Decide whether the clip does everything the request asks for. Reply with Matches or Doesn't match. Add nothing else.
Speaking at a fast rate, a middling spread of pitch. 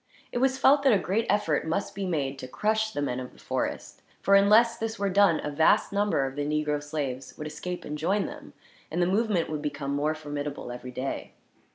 Doesn't match